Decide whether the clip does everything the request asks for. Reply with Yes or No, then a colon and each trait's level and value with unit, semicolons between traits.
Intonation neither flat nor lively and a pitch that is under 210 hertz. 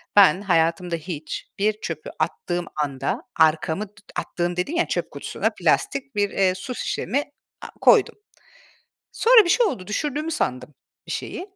No: wide, 8.9 semitones; high, 190 Hz